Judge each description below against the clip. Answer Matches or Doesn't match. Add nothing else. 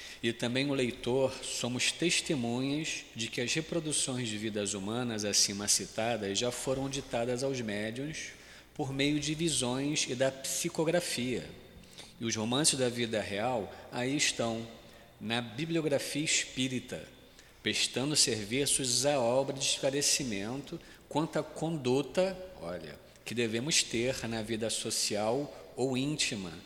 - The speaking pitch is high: Doesn't match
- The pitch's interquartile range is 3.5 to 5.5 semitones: Matches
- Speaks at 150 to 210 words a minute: Doesn't match